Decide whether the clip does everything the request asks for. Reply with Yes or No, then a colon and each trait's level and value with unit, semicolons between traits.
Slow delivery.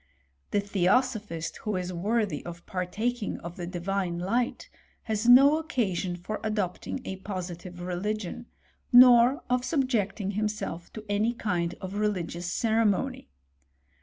Yes: slow, 130 wpm